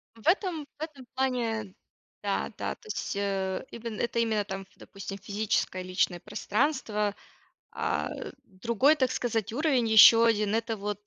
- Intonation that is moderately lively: Yes, average, 4.0 semitones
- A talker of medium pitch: No, high, 225 Hz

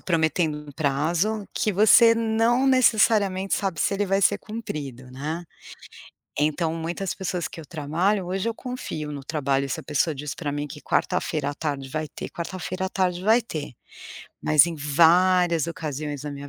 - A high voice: No, medium, 165 Hz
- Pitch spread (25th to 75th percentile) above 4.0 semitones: Yes, average, 4.8 semitones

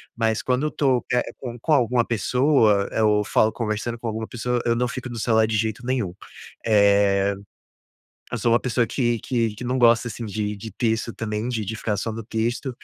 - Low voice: Yes, low, 115 Hz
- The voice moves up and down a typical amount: No, narrow, 2.2 semitones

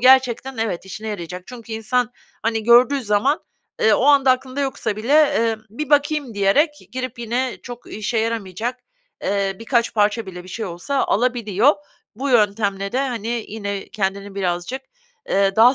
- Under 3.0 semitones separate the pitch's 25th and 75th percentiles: No, average, 4.0 semitones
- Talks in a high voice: Yes, high, 225 Hz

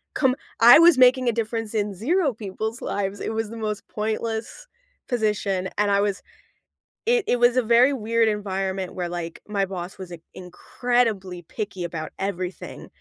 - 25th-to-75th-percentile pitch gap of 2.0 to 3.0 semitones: No, average, 3.8 semitones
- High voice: Yes, high, 215 Hz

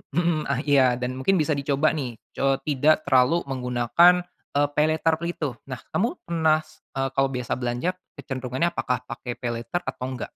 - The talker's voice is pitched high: No, medium, 140 Hz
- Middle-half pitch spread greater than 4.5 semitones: No, average, 3.8 semitones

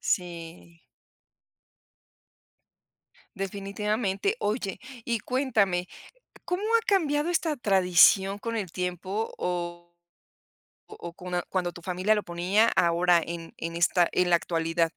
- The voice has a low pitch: No, medium, 185 Hz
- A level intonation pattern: No, average, 3.8 semitones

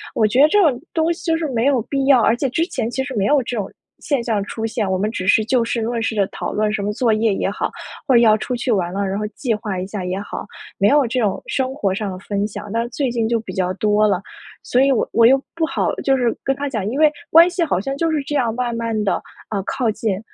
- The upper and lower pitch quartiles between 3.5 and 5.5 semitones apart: Yes, average, 4.4 semitones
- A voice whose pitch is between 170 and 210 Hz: No, high, 230 Hz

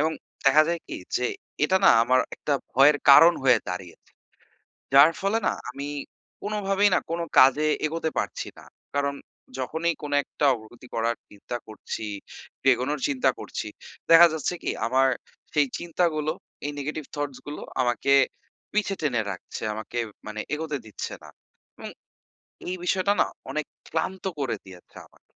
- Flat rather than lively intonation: No, average, 4.6 semitones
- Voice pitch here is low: No, medium, 145 Hz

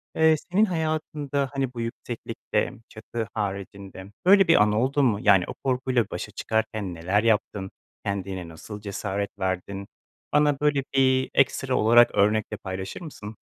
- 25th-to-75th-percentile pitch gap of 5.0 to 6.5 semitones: Yes, wide, 5.4 semitones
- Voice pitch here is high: No, low, 110 Hz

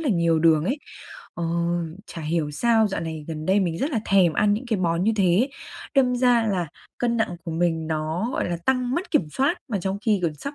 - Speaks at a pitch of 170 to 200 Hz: Yes, high, 190 Hz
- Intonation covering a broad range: Yes, wide, 6.3 semitones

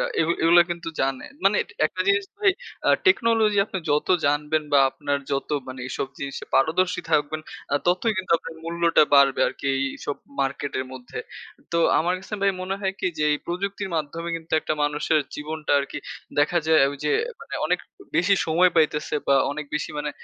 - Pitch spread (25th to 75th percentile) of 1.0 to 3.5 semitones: No, average, 3.9 semitones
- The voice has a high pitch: No, medium, 160 Hz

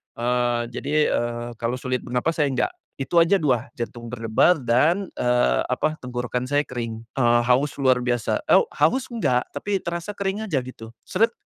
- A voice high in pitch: No, low, 125 Hz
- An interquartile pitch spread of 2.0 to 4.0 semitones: No, average, 5.0 semitones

